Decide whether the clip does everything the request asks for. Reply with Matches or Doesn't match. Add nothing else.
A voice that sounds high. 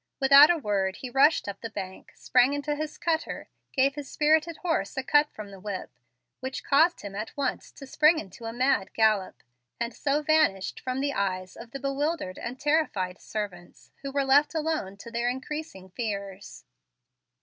Matches